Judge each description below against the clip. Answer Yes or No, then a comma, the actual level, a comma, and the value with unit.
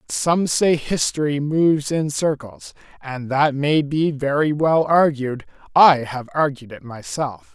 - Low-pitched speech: No, medium, 145 Hz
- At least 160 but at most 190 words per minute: No, average, 150 wpm